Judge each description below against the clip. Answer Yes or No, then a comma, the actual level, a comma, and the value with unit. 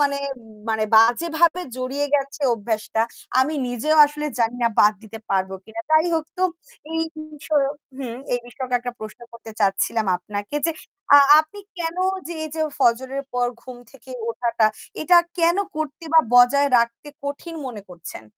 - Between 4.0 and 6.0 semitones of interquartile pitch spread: Yes, average, 5.2 semitones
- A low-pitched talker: No, very high, 255 Hz